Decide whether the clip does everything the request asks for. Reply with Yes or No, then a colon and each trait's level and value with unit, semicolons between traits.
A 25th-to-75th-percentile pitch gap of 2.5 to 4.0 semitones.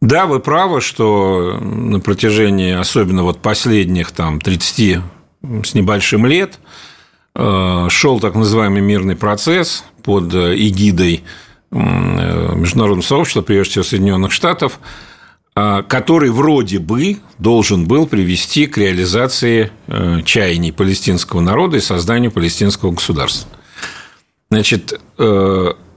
Yes: average, 3.7 semitones